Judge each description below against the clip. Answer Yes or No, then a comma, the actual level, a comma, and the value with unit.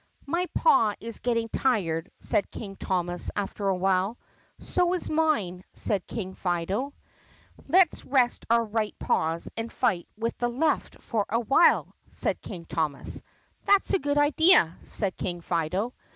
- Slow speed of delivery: No, average, 155 wpm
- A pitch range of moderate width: No, wide, 6.6 semitones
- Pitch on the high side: Yes, high, 220 Hz